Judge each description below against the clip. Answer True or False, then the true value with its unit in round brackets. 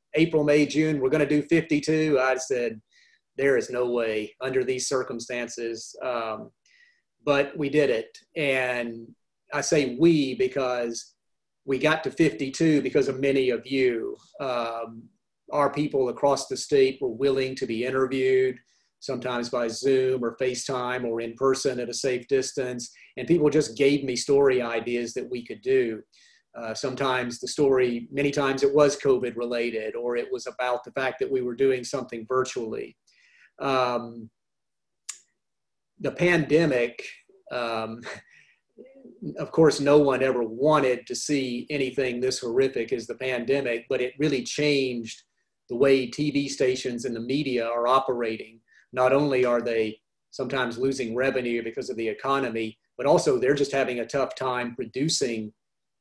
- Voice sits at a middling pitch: False (130 Hz)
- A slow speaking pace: False (155 wpm)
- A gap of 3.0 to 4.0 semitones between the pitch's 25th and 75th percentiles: True (3.3 semitones)